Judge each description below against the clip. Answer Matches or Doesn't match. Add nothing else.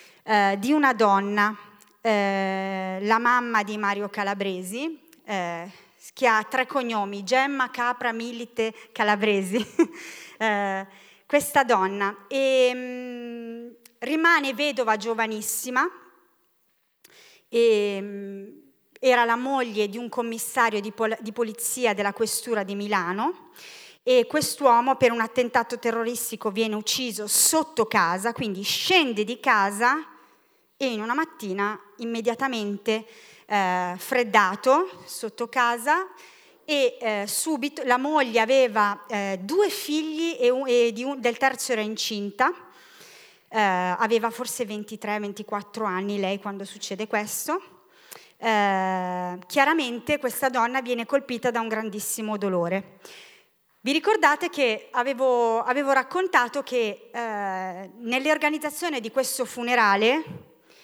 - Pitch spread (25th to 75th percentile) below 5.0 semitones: Matches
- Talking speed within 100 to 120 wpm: Matches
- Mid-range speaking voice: Doesn't match